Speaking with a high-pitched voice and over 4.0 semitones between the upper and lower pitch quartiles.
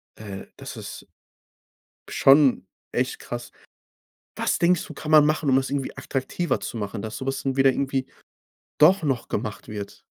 No: low, 135 Hz; average, 5.2 semitones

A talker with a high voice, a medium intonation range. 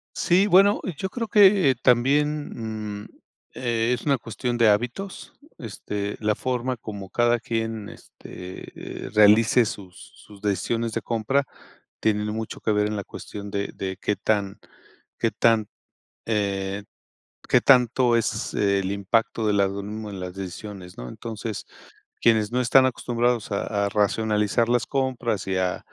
No: low, 110 Hz; average, 3.2 semitones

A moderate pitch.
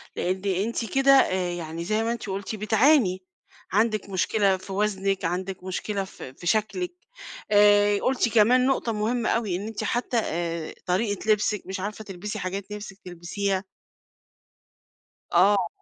No: high, 205 Hz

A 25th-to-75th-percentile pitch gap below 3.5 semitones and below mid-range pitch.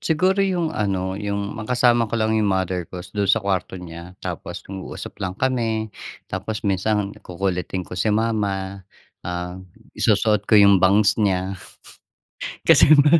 Yes: average, 2.8 semitones; low, 100 Hz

